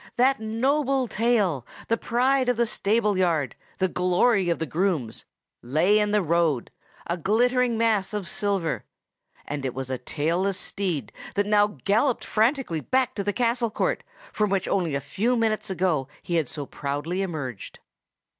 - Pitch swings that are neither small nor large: No, wide, 5.8 semitones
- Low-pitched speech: No, high, 195 Hz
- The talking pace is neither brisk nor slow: Yes, average, 165 wpm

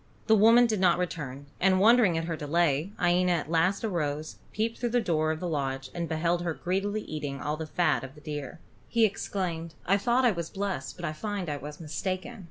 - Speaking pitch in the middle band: Yes, medium, 170 Hz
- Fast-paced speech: Yes, fast, 215 wpm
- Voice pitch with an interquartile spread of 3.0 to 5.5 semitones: Yes, average, 4.5 semitones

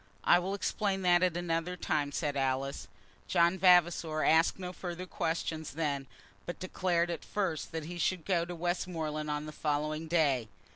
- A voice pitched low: No, medium, 170 Hz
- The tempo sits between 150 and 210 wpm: Yes, average, 165 wpm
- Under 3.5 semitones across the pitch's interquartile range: Yes, narrow, 2.6 semitones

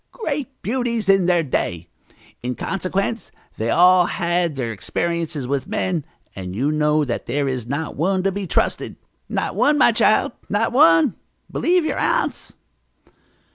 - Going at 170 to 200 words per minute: No, average, 145 wpm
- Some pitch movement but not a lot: No, wide, 6.4 semitones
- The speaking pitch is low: No, medium, 170 Hz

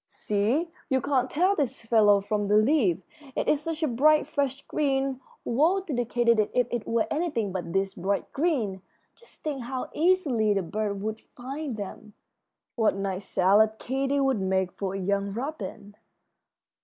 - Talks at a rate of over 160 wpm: Yes, average, 170 wpm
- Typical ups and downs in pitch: No, wide, 5.8 semitones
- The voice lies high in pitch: Yes, high, 235 Hz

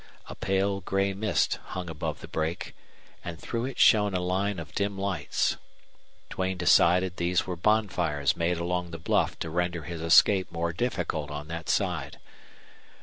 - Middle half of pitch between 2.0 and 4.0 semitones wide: Yes, average, 2.8 semitones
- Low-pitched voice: Yes, very low, 90 Hz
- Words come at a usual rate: Yes, average, 160 wpm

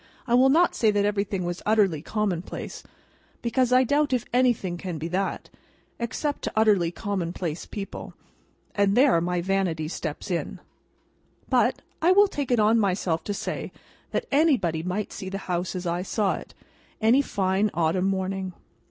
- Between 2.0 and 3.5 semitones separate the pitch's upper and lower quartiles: No, average, 4.7 semitones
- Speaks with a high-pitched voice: Yes, high, 195 Hz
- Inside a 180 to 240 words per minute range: No, average, 160 wpm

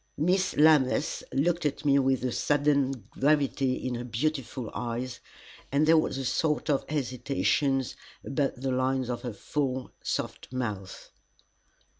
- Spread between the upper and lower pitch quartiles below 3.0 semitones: Yes, narrow, 2.5 semitones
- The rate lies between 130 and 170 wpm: Yes, average, 140 wpm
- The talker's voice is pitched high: No, low, 135 Hz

